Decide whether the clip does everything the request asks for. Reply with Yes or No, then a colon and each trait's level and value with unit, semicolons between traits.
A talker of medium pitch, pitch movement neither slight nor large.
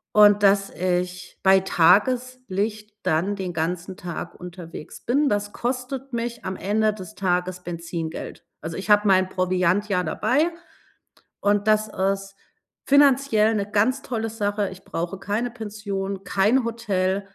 No: high, 200 Hz; average, 3.1 semitones